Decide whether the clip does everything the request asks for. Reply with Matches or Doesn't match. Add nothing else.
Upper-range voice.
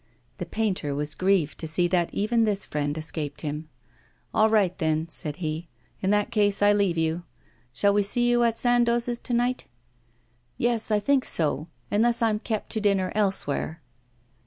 Matches